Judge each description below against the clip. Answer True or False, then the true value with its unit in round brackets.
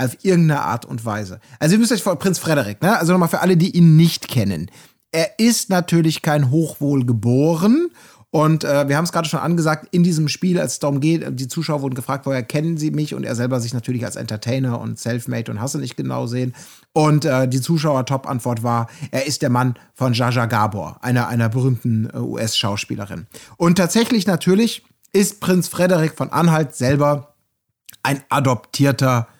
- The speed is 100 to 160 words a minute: False (190 wpm)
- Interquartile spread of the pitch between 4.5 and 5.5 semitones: True (5.1 semitones)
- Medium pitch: True (145 Hz)